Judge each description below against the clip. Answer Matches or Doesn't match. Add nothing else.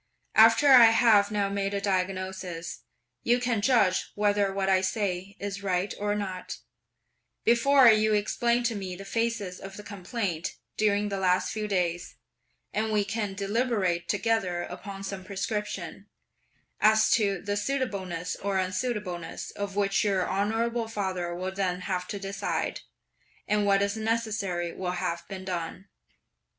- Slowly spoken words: Doesn't match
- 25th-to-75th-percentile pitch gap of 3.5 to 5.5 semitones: Doesn't match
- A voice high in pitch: Matches